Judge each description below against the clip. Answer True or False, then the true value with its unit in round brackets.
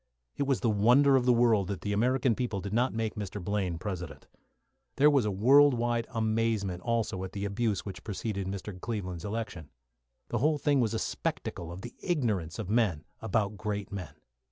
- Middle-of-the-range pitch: False (105 Hz)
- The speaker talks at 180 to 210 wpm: True (190 wpm)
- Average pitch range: True (3.5 semitones)